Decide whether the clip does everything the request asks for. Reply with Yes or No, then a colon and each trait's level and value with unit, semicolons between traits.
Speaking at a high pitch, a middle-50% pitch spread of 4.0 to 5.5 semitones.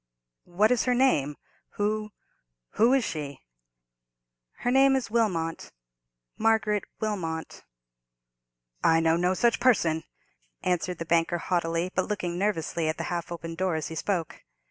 No: medium, 175 Hz; average, 4.7 semitones